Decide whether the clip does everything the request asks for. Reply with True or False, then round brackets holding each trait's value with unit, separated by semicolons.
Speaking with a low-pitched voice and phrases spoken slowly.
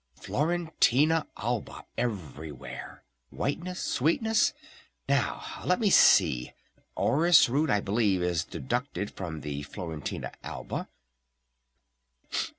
True (120 Hz; 90 wpm)